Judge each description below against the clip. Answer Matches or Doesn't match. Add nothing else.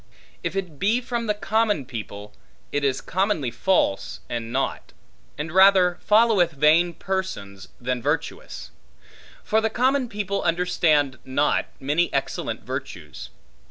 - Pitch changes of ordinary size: Doesn't match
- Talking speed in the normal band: Doesn't match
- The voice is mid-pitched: Matches